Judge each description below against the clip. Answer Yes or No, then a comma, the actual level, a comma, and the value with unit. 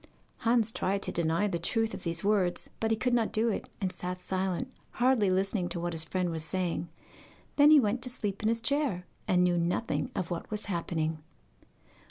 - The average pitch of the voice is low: No, high, 190 Hz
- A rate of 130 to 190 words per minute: No, fast, 205 wpm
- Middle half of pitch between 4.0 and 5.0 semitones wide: Yes, average, 4.4 semitones